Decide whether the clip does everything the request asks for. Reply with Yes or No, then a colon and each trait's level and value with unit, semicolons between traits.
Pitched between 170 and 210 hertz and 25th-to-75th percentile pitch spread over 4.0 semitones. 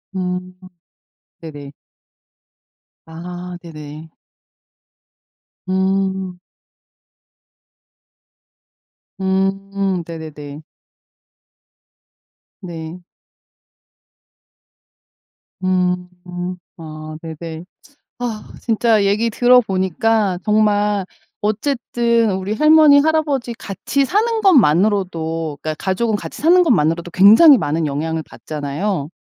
Yes: high, 190 Hz; wide, 5.5 semitones